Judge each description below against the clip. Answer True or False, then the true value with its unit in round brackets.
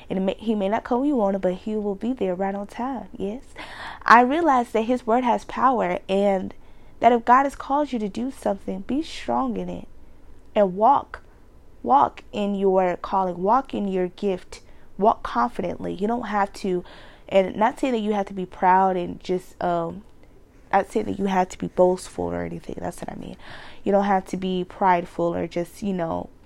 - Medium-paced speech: False (210 wpm)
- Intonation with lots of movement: False (3.8 semitones)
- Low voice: False (200 Hz)